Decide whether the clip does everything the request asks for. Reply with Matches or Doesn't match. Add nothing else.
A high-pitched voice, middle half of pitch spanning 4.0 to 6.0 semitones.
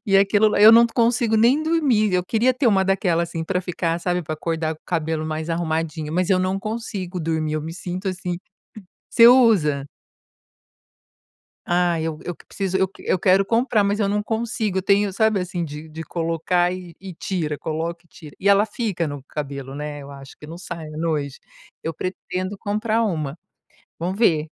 Doesn't match